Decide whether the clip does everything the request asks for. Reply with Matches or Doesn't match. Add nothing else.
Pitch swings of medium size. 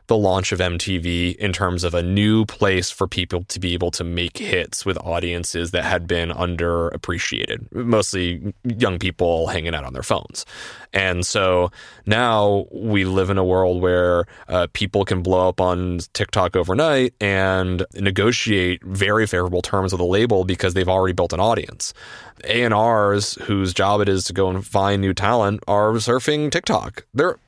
Doesn't match